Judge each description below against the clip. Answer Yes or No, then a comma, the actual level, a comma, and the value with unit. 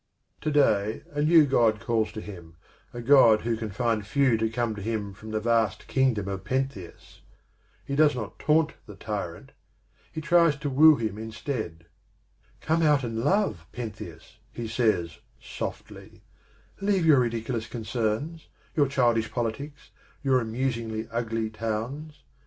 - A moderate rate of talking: Yes, average, 150 wpm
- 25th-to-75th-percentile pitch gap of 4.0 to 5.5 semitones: Yes, average, 4.4 semitones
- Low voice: Yes, low, 115 Hz